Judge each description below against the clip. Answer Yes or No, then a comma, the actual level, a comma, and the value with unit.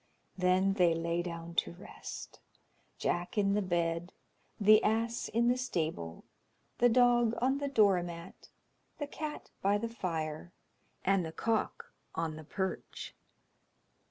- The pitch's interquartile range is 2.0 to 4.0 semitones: No, average, 5.3 semitones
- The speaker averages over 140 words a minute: No, slow, 135 wpm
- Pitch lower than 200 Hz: Yes, high, 190 Hz